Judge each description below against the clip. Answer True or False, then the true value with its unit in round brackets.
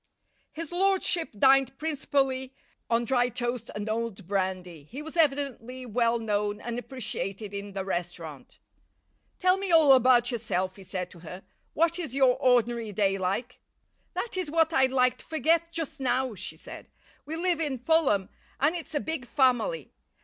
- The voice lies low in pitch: False (250 Hz)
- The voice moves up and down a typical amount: False (6.6 semitones)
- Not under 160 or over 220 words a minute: True (165 wpm)